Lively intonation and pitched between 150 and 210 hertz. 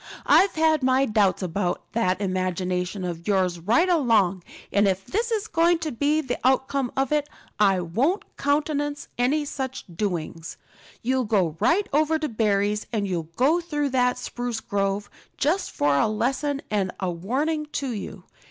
No: wide, 7.4 semitones; high, 240 Hz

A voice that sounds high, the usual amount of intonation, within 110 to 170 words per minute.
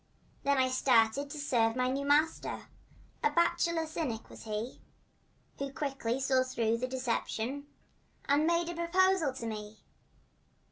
Yes: very high, 270 Hz; average, 4.7 semitones; average, 140 wpm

